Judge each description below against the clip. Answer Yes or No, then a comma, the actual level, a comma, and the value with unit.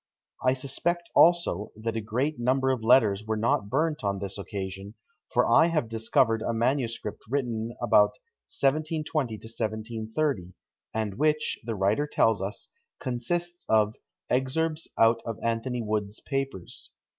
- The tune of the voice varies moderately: Yes, average, 4.2 semitones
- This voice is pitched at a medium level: No, low, 115 Hz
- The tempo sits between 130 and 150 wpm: Yes, average, 140 wpm